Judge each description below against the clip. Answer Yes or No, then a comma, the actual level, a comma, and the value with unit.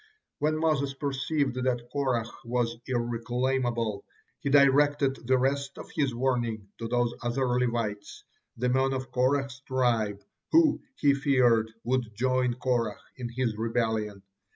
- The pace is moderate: No, slow, 130 wpm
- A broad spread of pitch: No, narrow, 2.4 semitones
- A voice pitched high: No, low, 125 Hz